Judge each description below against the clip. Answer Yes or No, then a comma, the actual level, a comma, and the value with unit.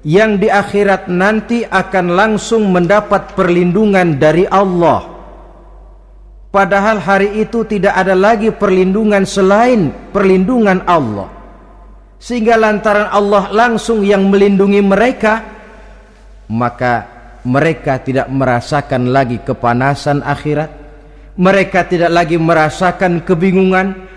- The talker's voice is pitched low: No, high, 190 Hz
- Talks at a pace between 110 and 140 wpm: No, average, 95 wpm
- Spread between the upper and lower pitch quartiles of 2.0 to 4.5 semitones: No, average, 5.1 semitones